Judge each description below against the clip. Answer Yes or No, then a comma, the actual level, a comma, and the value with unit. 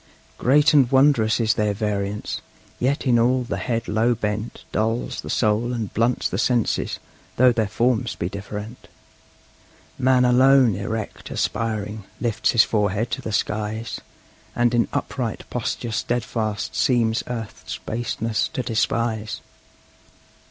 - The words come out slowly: Yes, slow, 130 wpm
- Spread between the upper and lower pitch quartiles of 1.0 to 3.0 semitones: Yes, narrow, 2.4 semitones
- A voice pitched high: No, low, 115 Hz